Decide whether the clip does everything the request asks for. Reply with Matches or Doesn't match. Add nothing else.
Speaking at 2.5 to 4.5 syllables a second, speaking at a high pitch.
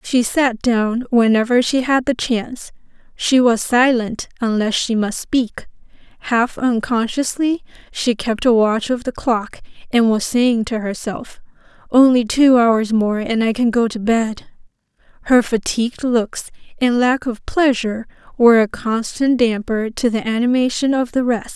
Matches